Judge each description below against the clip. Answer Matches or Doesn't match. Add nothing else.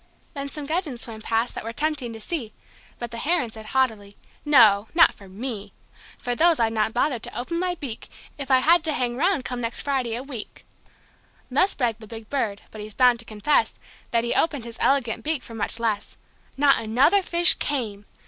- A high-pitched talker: Matches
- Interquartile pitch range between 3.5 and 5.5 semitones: Matches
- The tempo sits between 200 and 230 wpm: Matches